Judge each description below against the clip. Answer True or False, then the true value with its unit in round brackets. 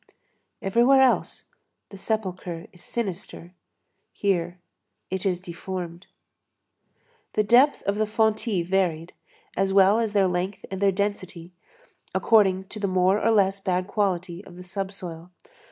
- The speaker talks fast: False (135 wpm)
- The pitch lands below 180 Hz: False (190 Hz)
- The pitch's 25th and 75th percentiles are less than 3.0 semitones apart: True (2.5 semitones)